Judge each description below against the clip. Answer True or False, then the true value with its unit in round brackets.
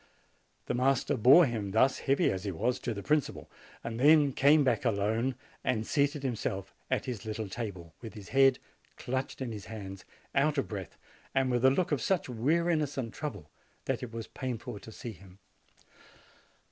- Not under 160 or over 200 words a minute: True (180 wpm)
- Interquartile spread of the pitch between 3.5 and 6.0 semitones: True (4.3 semitones)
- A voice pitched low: True (125 Hz)